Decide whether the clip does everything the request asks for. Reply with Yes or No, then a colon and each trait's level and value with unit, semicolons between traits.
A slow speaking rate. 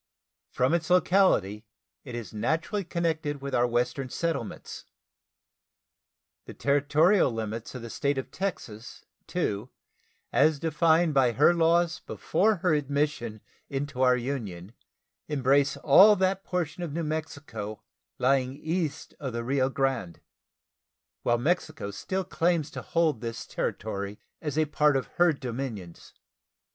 Yes: slow, 130 wpm